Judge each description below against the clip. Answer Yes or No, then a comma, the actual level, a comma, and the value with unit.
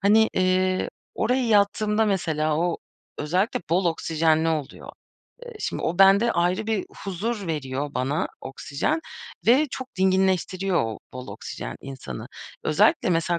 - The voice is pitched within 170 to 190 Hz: Yes, medium, 185 Hz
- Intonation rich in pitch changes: No, average, 4.6 semitones